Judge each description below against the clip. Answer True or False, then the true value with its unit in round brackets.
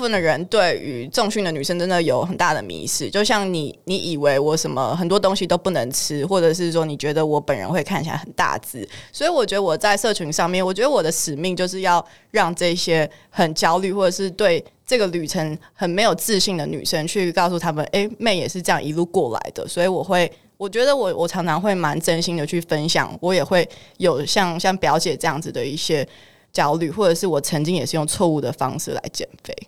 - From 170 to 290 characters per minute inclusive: False (330 characters per minute)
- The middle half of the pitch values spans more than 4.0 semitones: False (3.3 semitones)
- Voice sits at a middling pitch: True (175 Hz)